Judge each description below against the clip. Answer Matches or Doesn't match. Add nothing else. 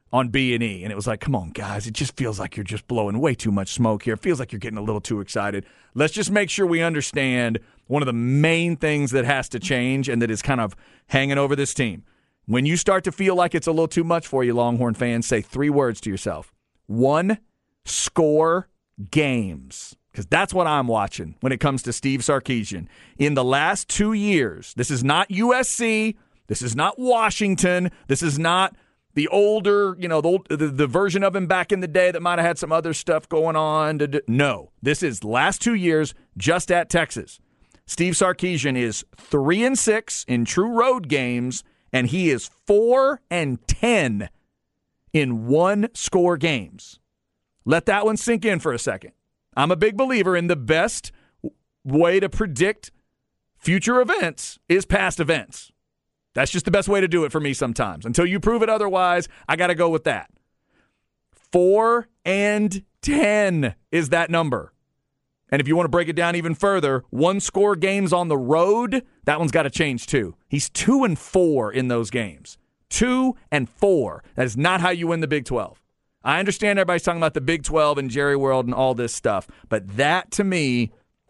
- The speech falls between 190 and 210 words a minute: Matches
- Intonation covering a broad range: Matches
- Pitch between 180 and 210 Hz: Doesn't match